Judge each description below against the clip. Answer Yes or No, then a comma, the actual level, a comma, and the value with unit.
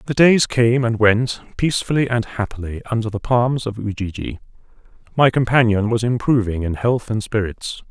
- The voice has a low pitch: Yes, low, 115 Hz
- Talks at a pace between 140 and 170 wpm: Yes, average, 160 wpm